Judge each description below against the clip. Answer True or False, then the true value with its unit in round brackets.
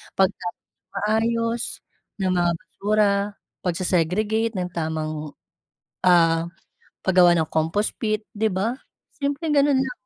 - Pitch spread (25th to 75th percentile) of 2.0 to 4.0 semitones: False (4.5 semitones)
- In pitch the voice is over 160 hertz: True (190 Hz)